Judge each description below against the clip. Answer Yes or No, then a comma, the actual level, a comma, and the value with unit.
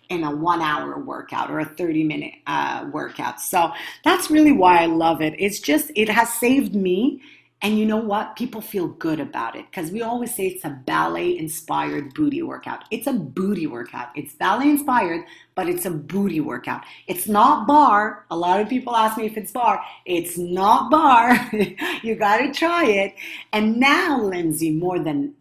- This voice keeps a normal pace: Yes, average, 190 wpm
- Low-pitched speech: No, high, 210 Hz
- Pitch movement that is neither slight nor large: No, wide, 7.4 semitones